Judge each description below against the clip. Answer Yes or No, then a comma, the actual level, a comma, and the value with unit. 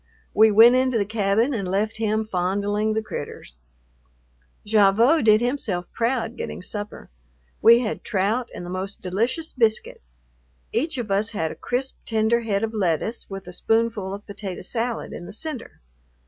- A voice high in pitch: Yes, high, 215 Hz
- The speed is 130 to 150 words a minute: No, average, 160 wpm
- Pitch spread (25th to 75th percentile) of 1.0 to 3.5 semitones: Yes, average, 2.9 semitones